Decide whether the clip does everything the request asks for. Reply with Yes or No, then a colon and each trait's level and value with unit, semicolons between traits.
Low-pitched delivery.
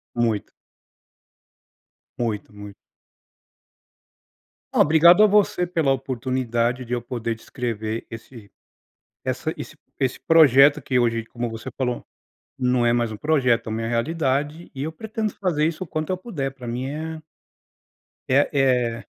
Yes: low, 130 Hz